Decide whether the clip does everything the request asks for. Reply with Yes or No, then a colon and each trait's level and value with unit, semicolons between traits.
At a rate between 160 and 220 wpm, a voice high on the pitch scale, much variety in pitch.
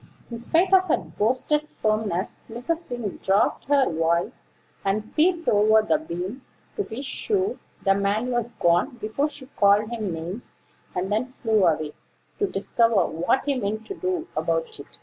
Yes: average, 165 wpm; high, 225 Hz; wide, 6.7 semitones